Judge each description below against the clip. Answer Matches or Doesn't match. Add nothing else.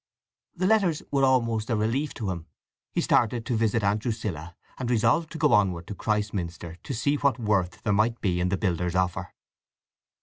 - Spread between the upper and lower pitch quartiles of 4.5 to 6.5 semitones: Matches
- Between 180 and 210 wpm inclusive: Matches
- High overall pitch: Doesn't match